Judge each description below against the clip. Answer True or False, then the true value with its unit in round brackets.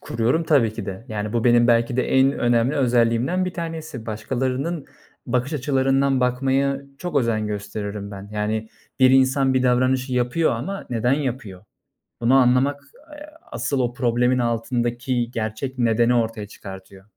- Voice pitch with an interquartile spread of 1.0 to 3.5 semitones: True (2.9 semitones)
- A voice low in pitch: True (125 Hz)